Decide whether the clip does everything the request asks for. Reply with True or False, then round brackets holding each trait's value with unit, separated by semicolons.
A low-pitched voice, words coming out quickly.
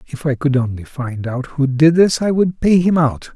False (145 Hz; 250 wpm)